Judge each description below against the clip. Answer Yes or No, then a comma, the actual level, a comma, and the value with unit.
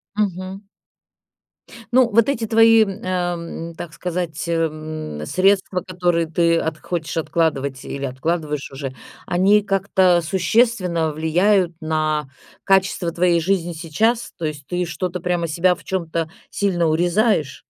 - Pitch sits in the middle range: Yes, medium, 175 Hz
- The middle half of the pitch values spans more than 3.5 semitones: No, average, 3.1 semitones